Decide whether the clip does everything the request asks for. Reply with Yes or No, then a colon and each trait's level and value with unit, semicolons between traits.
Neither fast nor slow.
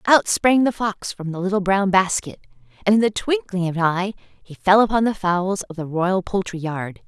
No: fast, 220 wpm